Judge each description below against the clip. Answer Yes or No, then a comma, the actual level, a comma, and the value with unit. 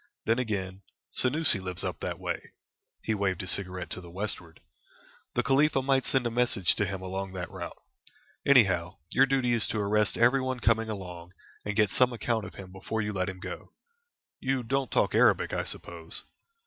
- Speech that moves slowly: No, average, 185 wpm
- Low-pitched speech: Yes, low, 105 Hz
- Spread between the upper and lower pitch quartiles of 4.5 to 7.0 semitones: Yes, average, 4.9 semitones